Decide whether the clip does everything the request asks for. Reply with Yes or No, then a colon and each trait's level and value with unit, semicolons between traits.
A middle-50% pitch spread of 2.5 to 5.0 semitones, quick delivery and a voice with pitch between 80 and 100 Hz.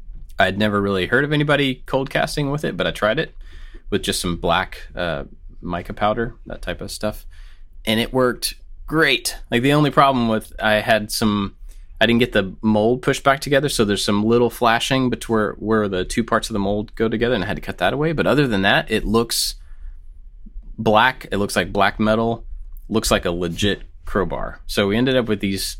No: average, 4.1 semitones; fast, 210 wpm; low, 110 Hz